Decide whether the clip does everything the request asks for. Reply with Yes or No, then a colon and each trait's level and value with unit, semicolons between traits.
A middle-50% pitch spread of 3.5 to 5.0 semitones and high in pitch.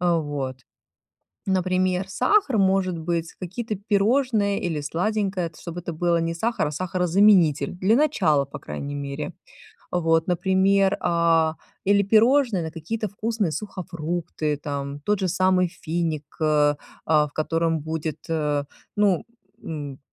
No: average, 3.9 semitones; medium, 175 Hz